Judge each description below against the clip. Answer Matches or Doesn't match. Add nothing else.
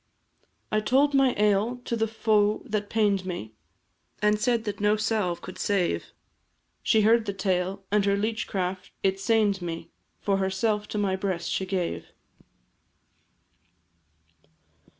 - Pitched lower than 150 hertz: Doesn't match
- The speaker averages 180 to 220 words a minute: Doesn't match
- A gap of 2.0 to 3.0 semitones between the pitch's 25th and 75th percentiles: Matches